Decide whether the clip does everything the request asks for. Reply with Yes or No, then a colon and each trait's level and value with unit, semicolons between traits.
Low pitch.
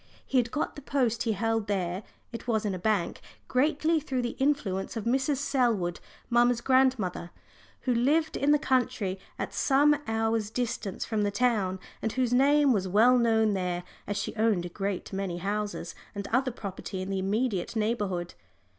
No: high, 225 Hz